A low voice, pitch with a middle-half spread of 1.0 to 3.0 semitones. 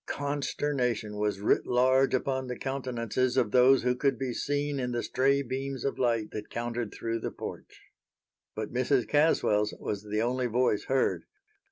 Yes: low, 125 Hz; average, 2.7 semitones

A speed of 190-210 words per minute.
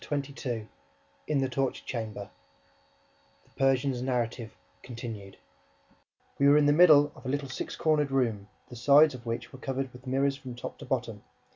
No: average, 170 wpm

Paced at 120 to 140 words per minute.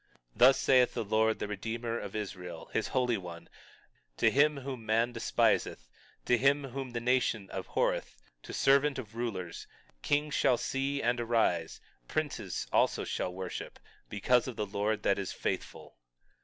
No: average, 155 wpm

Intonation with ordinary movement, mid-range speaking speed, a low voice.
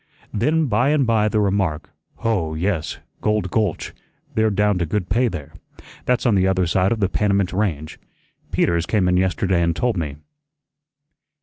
Yes: average, 3.7 semitones; average, 170 wpm; low, 100 Hz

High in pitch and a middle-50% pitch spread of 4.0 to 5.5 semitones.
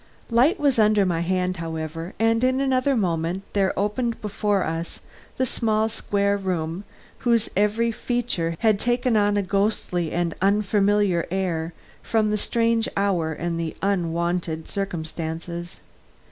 Yes: high, 200 Hz; average, 4.4 semitones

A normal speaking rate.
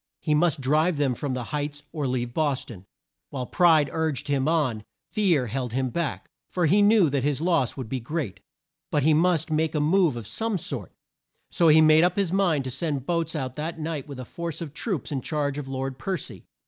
No: fast, 220 wpm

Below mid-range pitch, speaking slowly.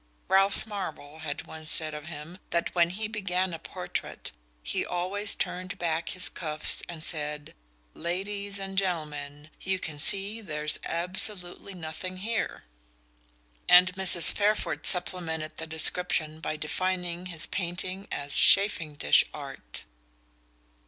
No: medium, 175 Hz; slow, 130 wpm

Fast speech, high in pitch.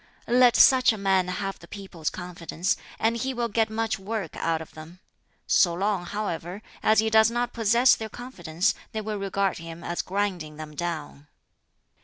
No: average, 175 wpm; high, 195 Hz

